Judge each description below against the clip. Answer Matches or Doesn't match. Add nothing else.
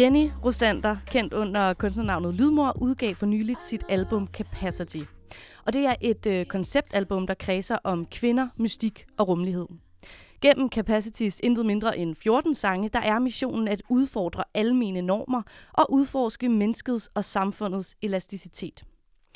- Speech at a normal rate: Doesn't match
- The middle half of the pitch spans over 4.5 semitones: Doesn't match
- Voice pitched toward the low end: Doesn't match